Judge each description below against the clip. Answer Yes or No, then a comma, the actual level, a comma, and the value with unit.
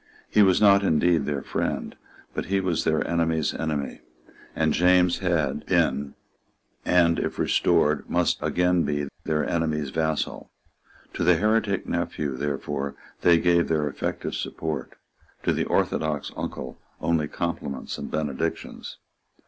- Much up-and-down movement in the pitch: No, average, 3.0 semitones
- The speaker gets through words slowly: Yes, slow, 130 wpm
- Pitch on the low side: Yes, very low, 80 Hz